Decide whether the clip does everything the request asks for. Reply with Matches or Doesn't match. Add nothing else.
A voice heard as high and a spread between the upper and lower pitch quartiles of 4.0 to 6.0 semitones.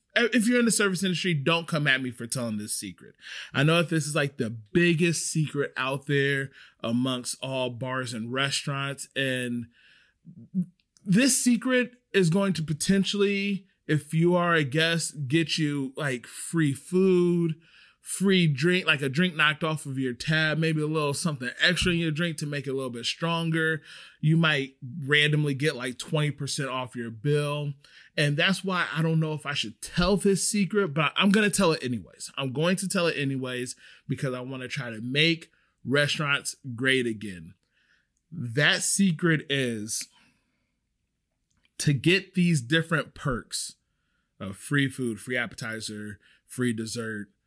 Doesn't match